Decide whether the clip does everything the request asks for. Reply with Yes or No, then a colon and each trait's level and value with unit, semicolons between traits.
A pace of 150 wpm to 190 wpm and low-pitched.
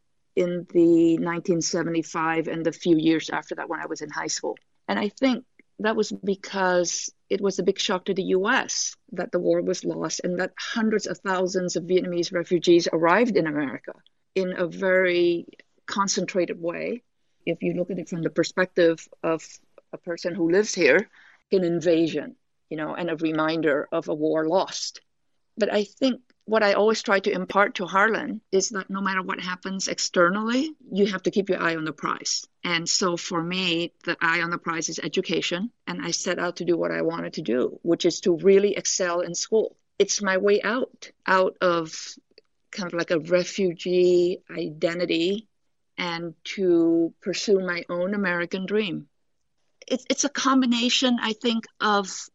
No: average, 180 wpm; medium, 180 Hz